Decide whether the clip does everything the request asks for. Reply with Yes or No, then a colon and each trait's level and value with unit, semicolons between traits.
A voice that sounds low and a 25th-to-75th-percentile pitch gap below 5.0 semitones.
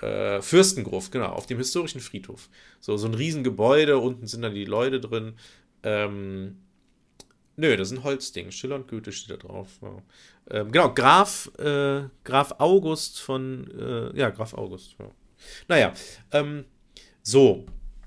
No: low, 125 Hz; average, 5.3 semitones